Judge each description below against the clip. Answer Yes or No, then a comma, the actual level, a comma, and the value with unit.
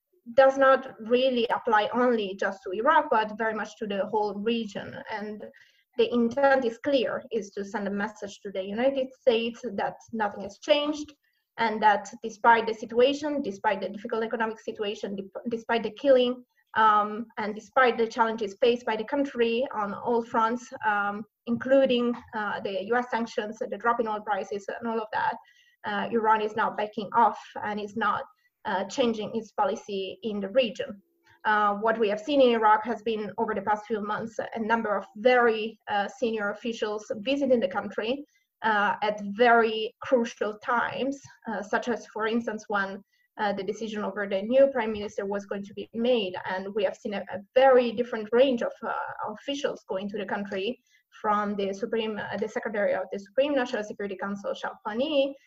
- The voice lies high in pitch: Yes, high, 225 Hz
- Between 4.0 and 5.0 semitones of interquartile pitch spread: No, average, 3.1 semitones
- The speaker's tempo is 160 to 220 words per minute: Yes, average, 180 wpm